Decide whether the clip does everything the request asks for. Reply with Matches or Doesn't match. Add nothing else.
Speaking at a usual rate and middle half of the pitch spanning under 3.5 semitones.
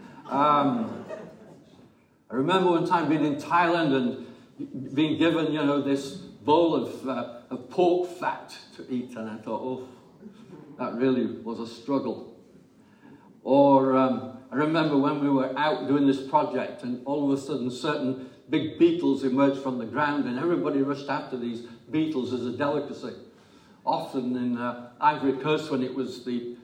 Matches